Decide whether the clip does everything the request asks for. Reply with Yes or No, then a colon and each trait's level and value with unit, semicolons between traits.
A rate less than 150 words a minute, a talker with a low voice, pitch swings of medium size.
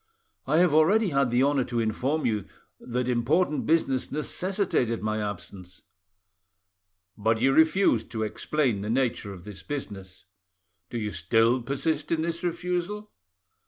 No: average, 140 wpm; low, 130 Hz; wide, 6.3 semitones